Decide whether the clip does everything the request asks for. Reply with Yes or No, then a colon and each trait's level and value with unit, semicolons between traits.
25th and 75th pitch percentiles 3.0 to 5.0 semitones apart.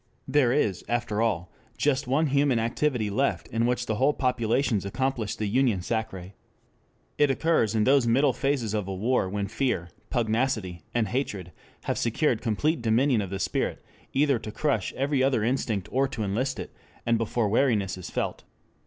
Yes: average, 4.2 semitones